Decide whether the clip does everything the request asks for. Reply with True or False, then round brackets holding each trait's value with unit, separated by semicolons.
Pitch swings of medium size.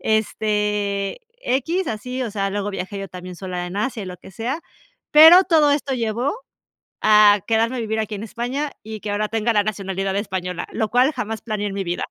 True (3.6 semitones)